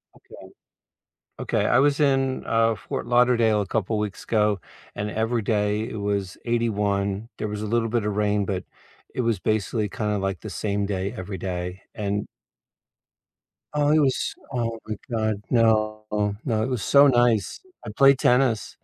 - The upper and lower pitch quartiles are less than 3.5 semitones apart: Yes, narrow, 2.5 semitones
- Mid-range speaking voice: No, low, 110 Hz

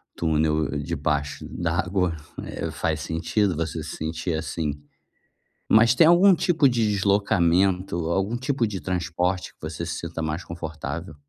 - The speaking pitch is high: No, very low, 85 Hz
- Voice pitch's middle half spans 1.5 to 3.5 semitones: No, average, 4.0 semitones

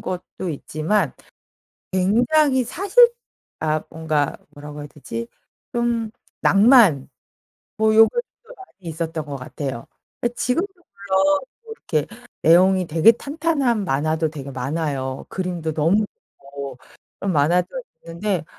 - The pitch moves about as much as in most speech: No, wide, 8.0 semitones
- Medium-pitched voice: Yes, medium, 180 Hz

